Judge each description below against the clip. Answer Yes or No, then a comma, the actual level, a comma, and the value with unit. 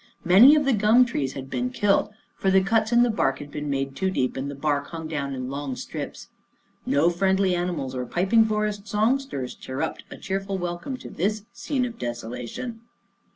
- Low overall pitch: No, medium, 185 Hz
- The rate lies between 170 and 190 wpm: No, average, 200 wpm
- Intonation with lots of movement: Yes, wide, 7.7 semitones